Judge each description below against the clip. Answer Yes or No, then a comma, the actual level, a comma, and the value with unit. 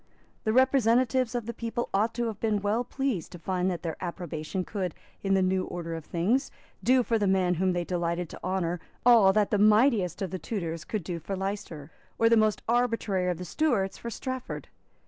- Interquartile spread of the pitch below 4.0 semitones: No, average, 4.4 semitones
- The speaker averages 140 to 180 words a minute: No, fast, 205 wpm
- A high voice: Yes, high, 195 Hz